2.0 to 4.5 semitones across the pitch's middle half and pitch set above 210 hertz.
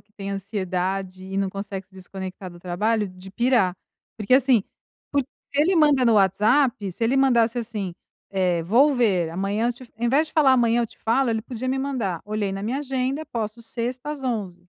No: average, 4.9 semitones; high, 220 Hz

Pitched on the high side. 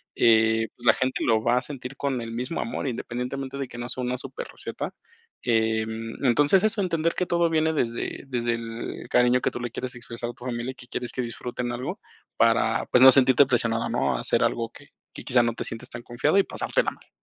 No: low, 125 Hz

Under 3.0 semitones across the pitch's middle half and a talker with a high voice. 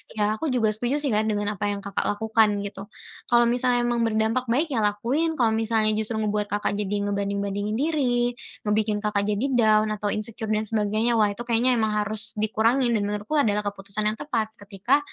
Yes: narrow, 2.5 semitones; high, 215 Hz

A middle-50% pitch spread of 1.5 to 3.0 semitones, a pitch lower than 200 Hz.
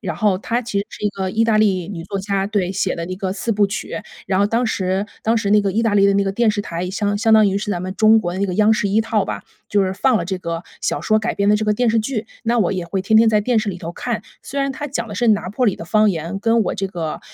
No: narrow, 2.6 semitones; high, 205 Hz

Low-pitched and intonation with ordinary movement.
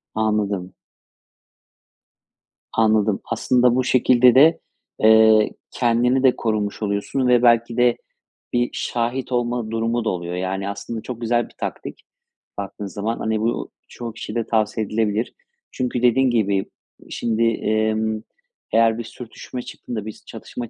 No: low, 115 Hz; narrow, 2.1 semitones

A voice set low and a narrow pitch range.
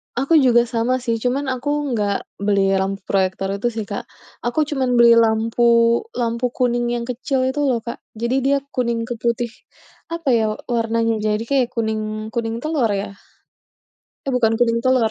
No: high, 235 Hz; narrow, 2.3 semitones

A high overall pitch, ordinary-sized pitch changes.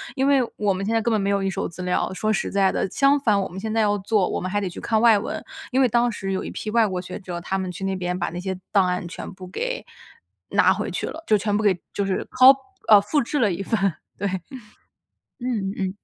Yes: high, 200 Hz; average, 3.1 semitones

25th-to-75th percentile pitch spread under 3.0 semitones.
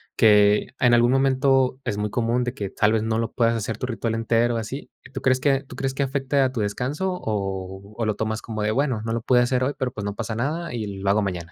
No: average, 3.4 semitones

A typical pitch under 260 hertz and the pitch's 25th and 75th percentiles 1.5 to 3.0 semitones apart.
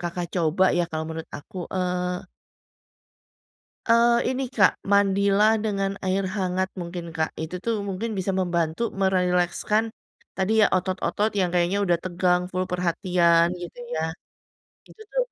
Yes: medium, 185 Hz; narrow, 2.4 semitones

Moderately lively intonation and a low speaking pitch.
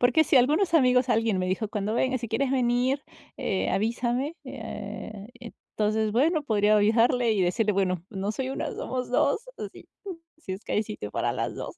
No: average, 3.6 semitones; high, 230 Hz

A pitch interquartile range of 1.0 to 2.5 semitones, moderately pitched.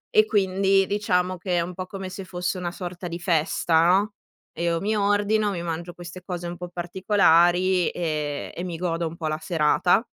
Yes: narrow, 2.1 semitones; medium, 180 Hz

